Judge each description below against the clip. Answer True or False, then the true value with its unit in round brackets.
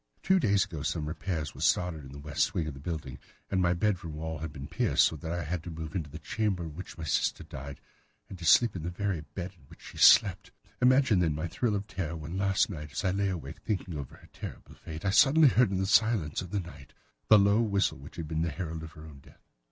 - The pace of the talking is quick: True (260 wpm)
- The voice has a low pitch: True (85 Hz)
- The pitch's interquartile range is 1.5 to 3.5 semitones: False (4.2 semitones)